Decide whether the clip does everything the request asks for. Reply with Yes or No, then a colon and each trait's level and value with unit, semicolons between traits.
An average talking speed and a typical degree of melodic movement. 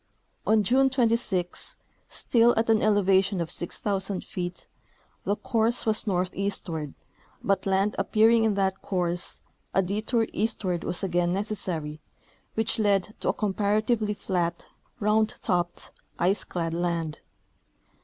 No: slow, 125 wpm; average, 3.4 semitones